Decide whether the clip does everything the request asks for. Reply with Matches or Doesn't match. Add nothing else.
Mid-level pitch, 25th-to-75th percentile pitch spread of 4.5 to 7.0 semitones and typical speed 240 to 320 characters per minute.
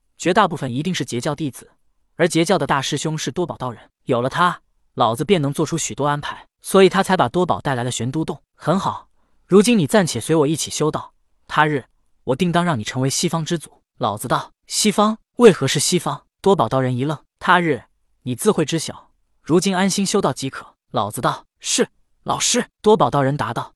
Matches